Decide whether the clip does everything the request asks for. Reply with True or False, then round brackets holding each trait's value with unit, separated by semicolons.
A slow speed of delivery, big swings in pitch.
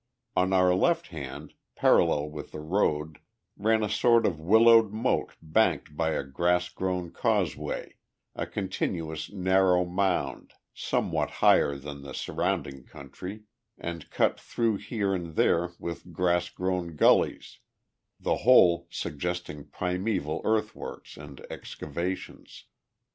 False (120 wpm; 3.7 semitones)